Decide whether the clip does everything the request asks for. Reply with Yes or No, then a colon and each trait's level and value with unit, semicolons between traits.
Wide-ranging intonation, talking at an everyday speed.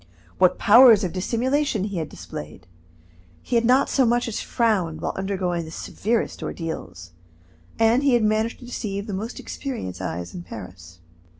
Yes: wide, 6.1 semitones; average, 165 wpm